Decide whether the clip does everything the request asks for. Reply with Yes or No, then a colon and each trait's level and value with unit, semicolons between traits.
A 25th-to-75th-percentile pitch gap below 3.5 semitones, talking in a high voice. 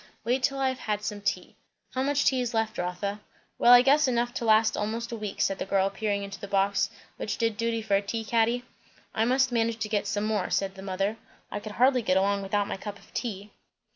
Yes: average, 2.9 semitones; high, 215 Hz